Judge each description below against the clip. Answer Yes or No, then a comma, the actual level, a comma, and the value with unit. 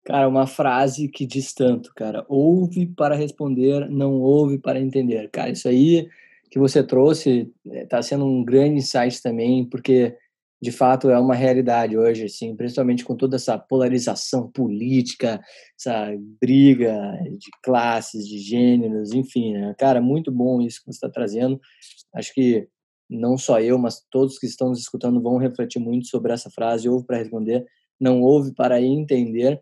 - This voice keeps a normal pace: Yes, average, 160 wpm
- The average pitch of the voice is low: Yes, low, 125 Hz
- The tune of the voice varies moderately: No, narrow, 2.0 semitones